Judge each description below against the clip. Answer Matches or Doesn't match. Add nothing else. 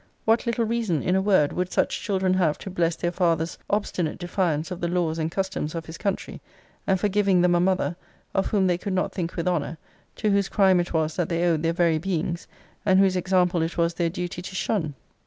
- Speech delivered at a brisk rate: Matches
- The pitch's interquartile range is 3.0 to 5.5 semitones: Doesn't match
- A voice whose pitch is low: Doesn't match